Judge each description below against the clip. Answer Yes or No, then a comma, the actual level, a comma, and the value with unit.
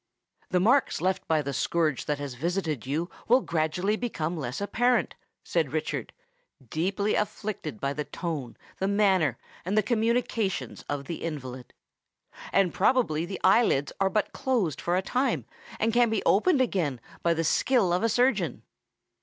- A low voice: No, medium, 185 Hz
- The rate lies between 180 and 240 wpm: No, average, 160 wpm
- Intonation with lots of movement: Yes, wide, 6.0 semitones